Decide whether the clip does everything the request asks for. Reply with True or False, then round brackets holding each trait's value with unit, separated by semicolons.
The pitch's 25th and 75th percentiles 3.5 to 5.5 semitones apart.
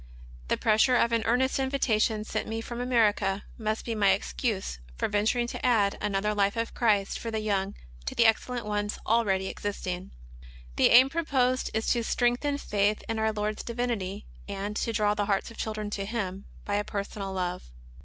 False (2.6 semitones)